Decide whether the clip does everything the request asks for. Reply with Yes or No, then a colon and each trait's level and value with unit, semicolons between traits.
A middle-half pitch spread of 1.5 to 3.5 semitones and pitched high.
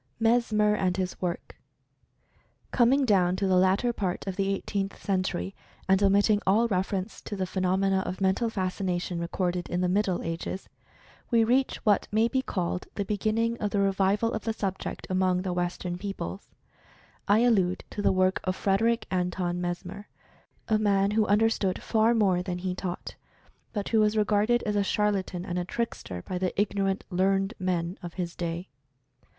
Yes: narrow, 2.5 semitones; high, 195 Hz